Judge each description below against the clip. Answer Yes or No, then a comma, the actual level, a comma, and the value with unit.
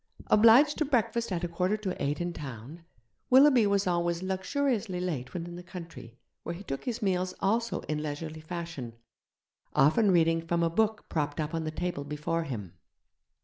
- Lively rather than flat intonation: No, average, 4.8 semitones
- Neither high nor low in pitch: Yes, medium, 175 Hz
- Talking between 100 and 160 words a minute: No, average, 180 wpm